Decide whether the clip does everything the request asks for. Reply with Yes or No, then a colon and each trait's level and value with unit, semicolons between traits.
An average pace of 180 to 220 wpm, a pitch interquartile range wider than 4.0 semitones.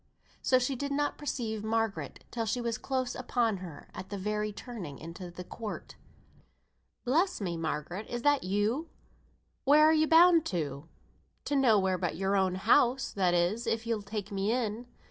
No: average, 170 wpm; average, 5.2 semitones